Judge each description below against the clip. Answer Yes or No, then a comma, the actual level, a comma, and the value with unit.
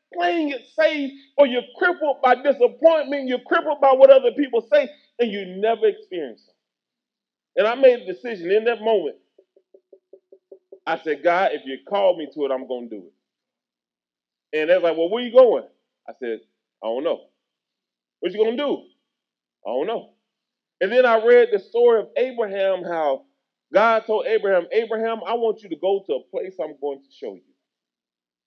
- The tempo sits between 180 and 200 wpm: Yes, average, 190 wpm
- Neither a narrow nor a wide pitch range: No, wide, 7.8 semitones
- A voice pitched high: Yes, high, 240 Hz